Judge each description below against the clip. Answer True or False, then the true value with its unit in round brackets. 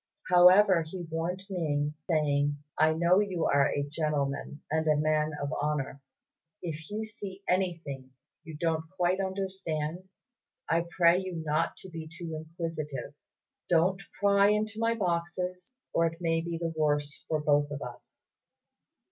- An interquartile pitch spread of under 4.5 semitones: True (3.2 semitones)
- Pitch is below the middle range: False (165 Hz)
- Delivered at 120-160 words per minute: True (150 wpm)